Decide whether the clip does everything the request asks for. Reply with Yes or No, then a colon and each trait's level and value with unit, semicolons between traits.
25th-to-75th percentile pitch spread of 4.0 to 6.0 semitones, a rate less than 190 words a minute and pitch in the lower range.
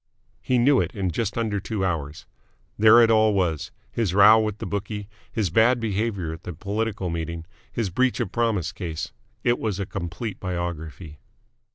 Yes: average, 4.3 semitones; average, 175 wpm; low, 100 Hz